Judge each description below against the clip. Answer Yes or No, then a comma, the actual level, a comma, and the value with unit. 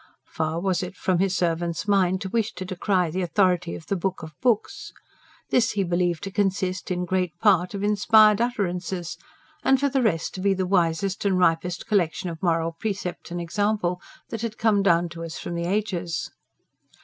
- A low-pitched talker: No, medium, 185 Hz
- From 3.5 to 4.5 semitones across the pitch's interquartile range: No, average, 2.7 semitones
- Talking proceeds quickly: No, average, 190 wpm